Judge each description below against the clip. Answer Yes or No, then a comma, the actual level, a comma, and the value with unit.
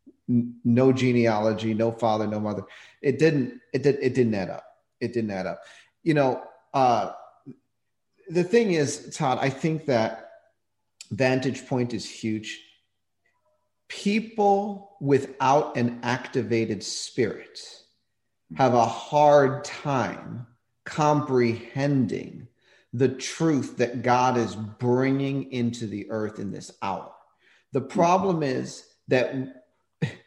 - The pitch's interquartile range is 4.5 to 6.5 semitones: No, average, 3.8 semitones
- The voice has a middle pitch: No, low, 125 Hz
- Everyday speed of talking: No, slow, 115 wpm